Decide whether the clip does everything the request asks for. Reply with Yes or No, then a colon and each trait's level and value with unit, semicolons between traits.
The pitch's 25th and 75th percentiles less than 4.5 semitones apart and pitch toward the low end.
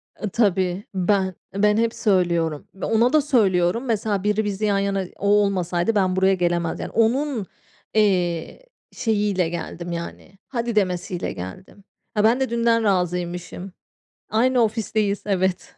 No: average, 3.6 semitones; high, 200 Hz